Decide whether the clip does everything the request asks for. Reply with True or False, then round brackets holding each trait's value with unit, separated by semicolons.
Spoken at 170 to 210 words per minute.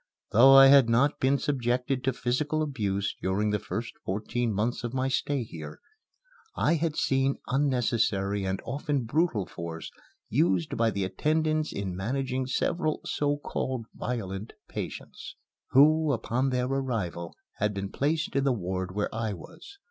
False (150 wpm)